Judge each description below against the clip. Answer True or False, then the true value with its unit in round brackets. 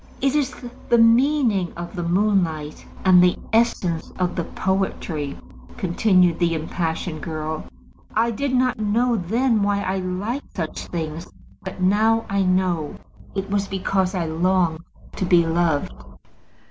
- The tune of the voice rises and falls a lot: False (4.1 semitones)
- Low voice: False (185 Hz)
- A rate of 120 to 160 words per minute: True (140 wpm)